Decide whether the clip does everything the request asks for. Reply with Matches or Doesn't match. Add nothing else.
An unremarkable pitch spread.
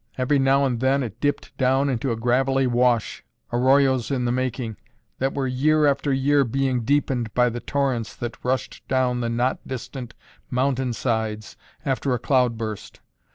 Doesn't match